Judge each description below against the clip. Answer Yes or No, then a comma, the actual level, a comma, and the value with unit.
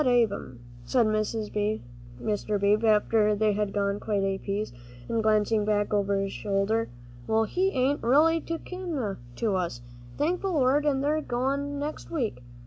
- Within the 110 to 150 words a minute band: No, average, 165 wpm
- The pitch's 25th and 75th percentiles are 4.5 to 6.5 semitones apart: Yes, average, 5.2 semitones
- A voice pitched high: Yes, high, 215 Hz